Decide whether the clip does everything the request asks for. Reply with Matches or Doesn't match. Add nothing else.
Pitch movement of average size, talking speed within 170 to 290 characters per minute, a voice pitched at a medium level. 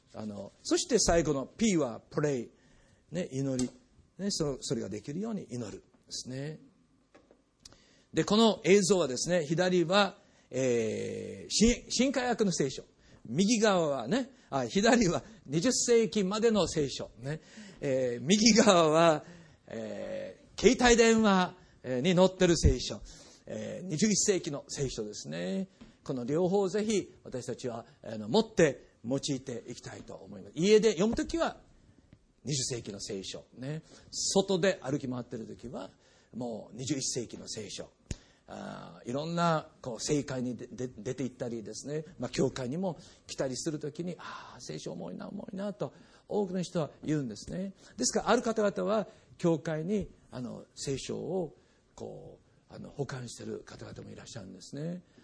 Doesn't match